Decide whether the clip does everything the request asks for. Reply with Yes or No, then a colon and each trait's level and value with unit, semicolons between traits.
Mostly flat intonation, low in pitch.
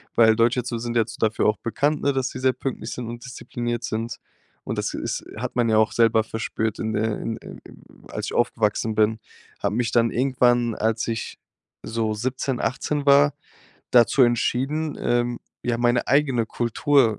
Yes: narrow, 2.3 semitones; low, 120 Hz